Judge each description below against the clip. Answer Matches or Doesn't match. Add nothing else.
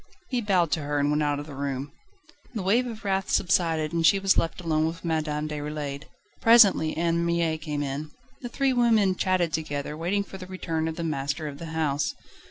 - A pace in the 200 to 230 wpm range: Matches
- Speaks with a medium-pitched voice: Matches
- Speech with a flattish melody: Doesn't match